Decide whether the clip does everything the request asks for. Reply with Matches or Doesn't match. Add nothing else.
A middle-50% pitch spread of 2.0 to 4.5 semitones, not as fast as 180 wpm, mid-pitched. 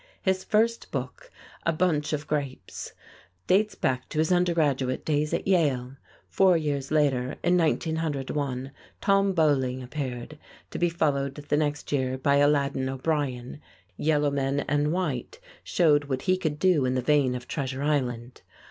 Matches